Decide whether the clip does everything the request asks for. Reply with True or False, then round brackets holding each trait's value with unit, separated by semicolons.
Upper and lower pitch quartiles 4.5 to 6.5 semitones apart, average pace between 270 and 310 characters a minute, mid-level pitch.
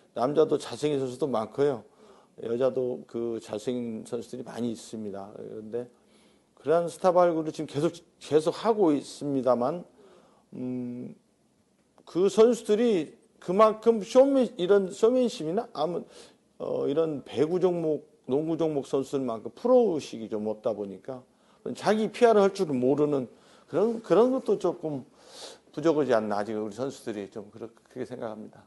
False (7.8 semitones; 295 characters per minute; 145 Hz)